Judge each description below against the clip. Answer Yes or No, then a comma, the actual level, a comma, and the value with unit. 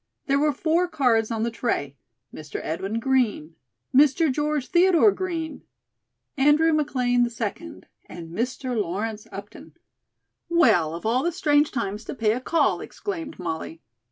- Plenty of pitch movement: Yes, wide, 6.5 semitones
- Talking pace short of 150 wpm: Yes, average, 140 wpm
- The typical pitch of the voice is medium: No, very high, 250 Hz